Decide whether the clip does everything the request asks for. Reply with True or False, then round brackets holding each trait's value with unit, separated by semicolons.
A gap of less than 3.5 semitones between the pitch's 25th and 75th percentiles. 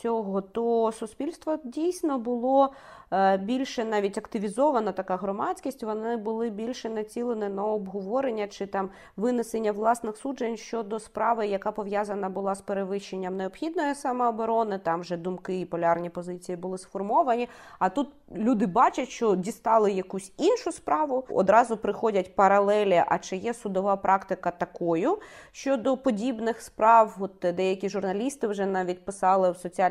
False (3.8 semitones)